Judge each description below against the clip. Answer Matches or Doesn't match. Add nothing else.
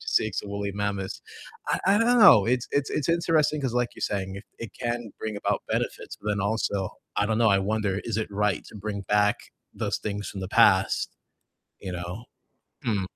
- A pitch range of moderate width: Matches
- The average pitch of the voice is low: Matches